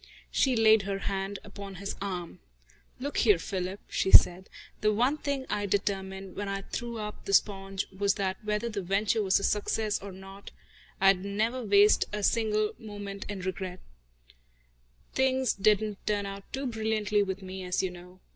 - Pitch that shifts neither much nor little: No, narrow, 1.8 semitones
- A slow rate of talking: No, average, 170 wpm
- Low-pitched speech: No, high, 200 Hz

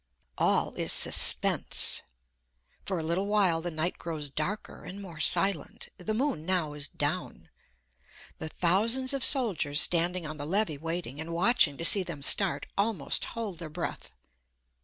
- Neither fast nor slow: Yes, average, 155 wpm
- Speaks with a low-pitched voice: No, medium, 175 Hz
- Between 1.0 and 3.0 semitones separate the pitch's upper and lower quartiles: No, average, 4.3 semitones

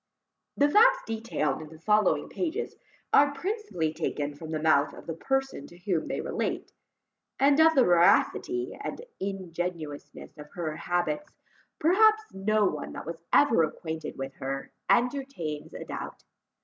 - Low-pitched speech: No, medium, 185 Hz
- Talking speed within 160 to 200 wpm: No, average, 150 wpm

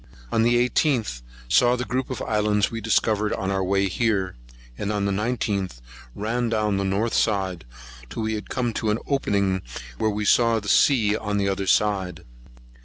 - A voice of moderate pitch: No, low, 105 Hz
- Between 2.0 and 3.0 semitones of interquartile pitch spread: Yes, average, 2.7 semitones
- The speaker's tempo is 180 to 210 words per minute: Yes, average, 185 wpm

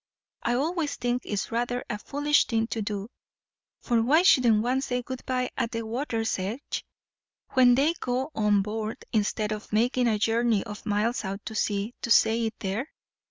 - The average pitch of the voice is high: Yes, high, 230 Hz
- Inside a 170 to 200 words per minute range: Yes, average, 180 wpm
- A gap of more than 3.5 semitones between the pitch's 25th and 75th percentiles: No, average, 2.9 semitones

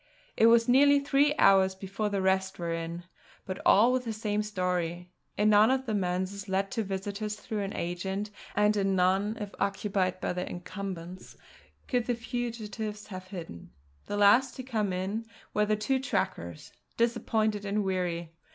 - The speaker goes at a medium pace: Yes, average, 170 wpm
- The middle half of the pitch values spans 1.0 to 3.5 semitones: Yes, average, 2.9 semitones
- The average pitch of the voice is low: No, high, 205 Hz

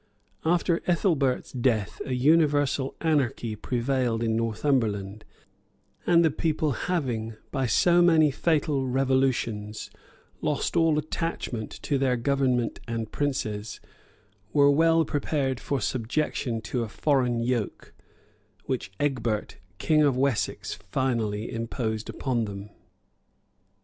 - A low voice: Yes, low, 130 Hz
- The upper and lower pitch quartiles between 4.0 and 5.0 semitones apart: Yes, average, 4.4 semitones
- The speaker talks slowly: Yes, slow, 110 wpm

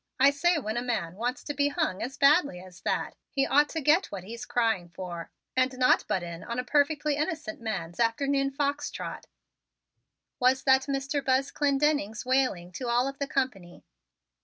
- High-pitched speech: Yes, very high, 260 Hz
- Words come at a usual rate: Yes, average, 185 wpm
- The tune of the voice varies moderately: Yes, average, 4.5 semitones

